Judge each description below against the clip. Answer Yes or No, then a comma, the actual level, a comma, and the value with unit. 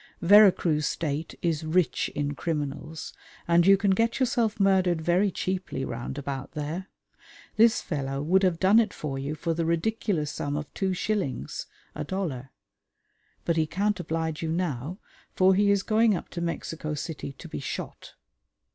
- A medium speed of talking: Yes, average, 165 wpm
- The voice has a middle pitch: Yes, medium, 170 Hz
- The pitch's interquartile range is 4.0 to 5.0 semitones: Yes, average, 4.3 semitones